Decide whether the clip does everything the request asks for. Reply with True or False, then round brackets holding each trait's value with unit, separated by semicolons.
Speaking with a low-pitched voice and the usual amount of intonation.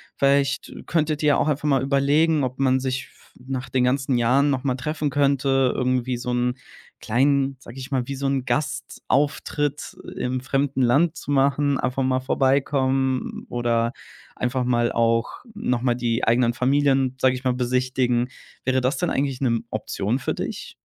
False (130 Hz; 1.9 semitones)